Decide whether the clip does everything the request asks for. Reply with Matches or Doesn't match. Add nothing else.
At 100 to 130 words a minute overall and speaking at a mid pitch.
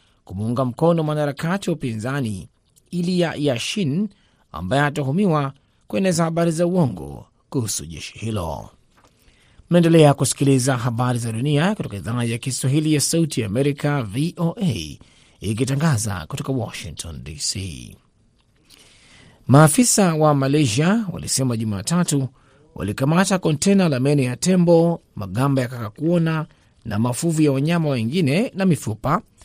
Matches